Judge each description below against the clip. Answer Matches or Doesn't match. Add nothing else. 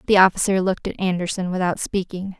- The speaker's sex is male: Doesn't match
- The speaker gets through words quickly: Doesn't match